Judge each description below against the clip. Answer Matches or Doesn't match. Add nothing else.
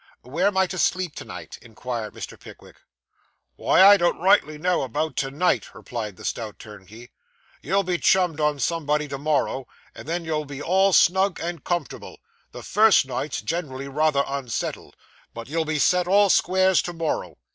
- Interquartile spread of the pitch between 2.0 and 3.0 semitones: Doesn't match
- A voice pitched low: Doesn't match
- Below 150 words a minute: Doesn't match